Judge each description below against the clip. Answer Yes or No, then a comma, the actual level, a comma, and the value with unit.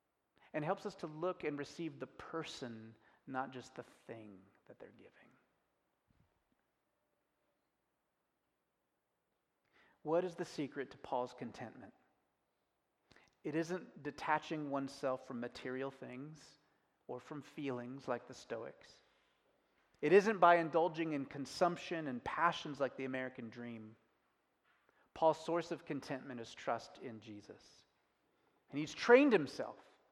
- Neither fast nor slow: No, slow, 120 wpm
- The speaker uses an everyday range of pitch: Yes, average, 4.4 semitones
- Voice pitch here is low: No, medium, 145 Hz